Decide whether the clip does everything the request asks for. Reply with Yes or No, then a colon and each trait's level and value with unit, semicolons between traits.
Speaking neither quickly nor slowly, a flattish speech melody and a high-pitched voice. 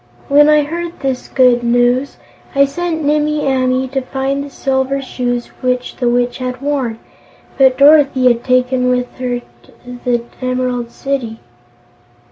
Yes: average, 150 wpm; narrow, 2.0 semitones; very high, 255 Hz